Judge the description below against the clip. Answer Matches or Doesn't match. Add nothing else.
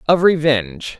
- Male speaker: Matches